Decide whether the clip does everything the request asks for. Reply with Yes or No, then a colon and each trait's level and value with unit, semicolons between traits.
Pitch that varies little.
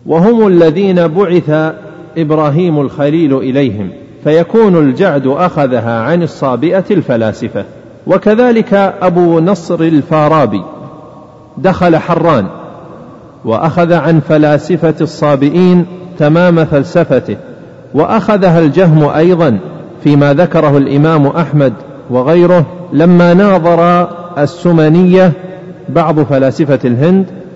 No: average, 3.0 semitones